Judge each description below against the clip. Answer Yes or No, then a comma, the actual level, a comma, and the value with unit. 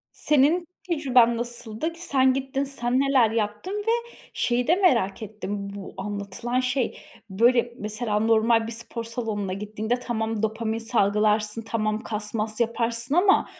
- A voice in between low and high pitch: No, high, 230 Hz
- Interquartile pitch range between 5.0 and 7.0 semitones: No, average, 3.1 semitones